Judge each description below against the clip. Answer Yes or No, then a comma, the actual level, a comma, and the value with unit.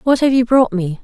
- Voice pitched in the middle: No, high, 235 Hz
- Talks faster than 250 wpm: Yes, fast, 290 wpm